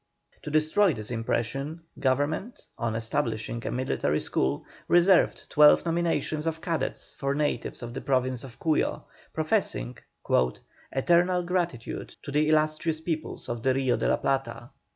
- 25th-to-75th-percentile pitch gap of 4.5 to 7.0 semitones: Yes, average, 5.0 semitones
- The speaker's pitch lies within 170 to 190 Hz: No, medium, 145 Hz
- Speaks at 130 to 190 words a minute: Yes, average, 140 wpm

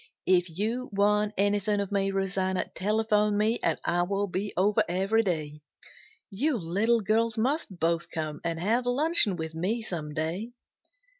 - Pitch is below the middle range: No, high, 200 Hz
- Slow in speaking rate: No, average, 155 wpm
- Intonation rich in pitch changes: No, average, 3.7 semitones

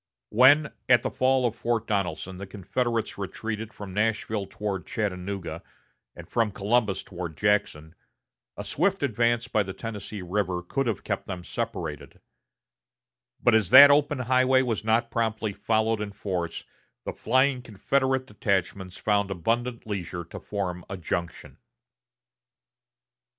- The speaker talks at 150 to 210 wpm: No, slow, 135 wpm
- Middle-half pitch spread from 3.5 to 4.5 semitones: Yes, average, 3.8 semitones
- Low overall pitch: Yes, low, 105 Hz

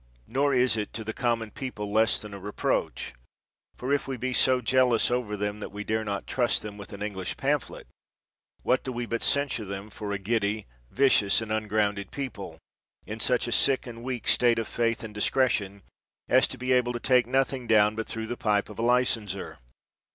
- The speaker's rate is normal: No, fast, 210 wpm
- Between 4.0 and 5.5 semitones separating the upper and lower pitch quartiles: No, average, 3.3 semitones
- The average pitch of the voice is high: No, low, 115 Hz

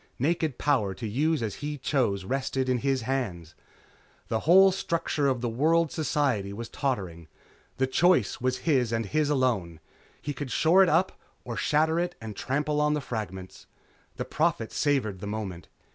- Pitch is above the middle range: No, low, 130 Hz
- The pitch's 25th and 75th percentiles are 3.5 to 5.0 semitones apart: No, wide, 5.5 semitones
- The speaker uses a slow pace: No, average, 165 wpm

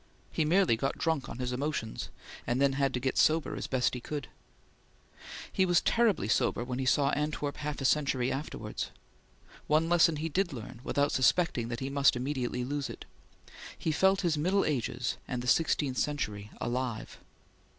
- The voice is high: No, medium, 140 Hz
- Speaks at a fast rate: No, average, 175 wpm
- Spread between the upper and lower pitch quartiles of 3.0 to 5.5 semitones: Yes, average, 3.9 semitones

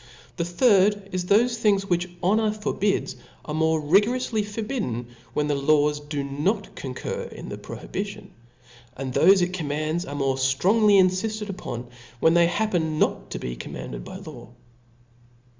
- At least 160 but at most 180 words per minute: Yes, average, 165 wpm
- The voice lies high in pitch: No, medium, 175 Hz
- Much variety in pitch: Yes, wide, 5.9 semitones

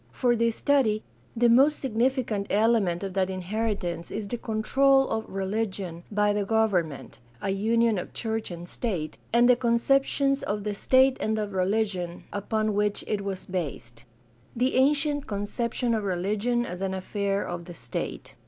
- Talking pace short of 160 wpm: No, average, 170 wpm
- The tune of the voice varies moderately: Yes, average, 3.8 semitones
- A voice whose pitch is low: No, high, 210 Hz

